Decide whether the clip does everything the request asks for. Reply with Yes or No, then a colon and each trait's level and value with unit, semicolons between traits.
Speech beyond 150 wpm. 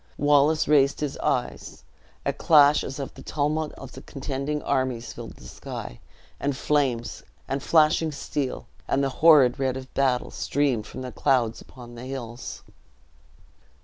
No: average, 145 wpm